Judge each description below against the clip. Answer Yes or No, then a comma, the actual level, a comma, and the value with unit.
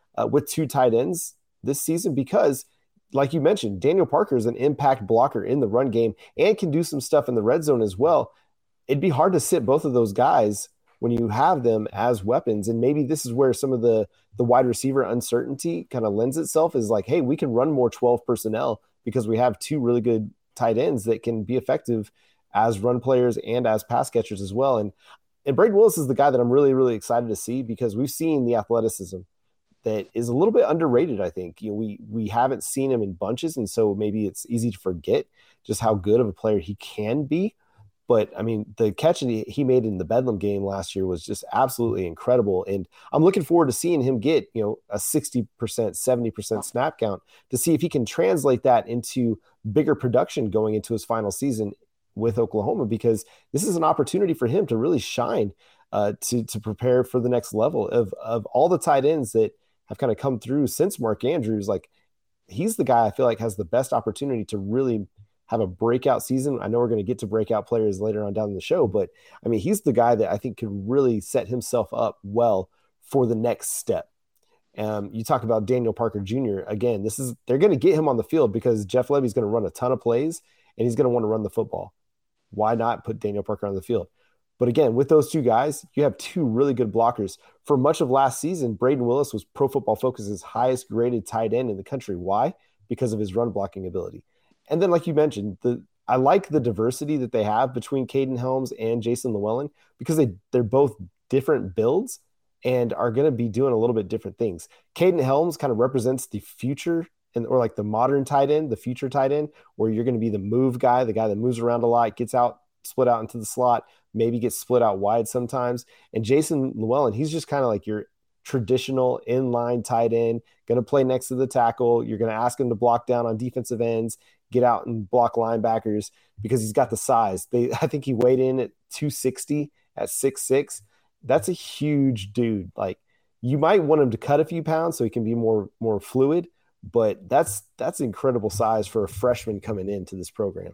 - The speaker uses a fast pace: Yes, fast, 225 wpm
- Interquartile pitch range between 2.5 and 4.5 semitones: Yes, average, 3.5 semitones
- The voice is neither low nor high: No, low, 120 Hz